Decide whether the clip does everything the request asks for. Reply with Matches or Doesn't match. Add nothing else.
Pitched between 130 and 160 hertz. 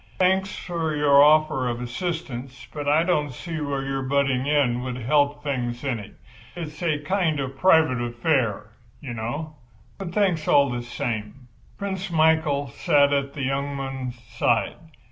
Matches